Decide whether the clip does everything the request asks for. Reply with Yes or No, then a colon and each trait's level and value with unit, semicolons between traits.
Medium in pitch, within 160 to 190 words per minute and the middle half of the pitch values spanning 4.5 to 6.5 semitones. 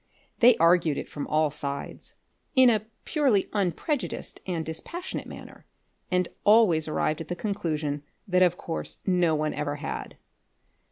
No: medium, 175 Hz; average, 145 wpm; average, 5.1 semitones